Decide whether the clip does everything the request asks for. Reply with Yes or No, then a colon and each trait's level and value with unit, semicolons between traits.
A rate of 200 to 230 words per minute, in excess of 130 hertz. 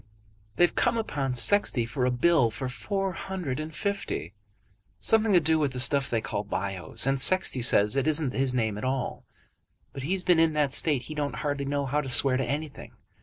Yes: fast, 205 wpm; medium, 140 Hz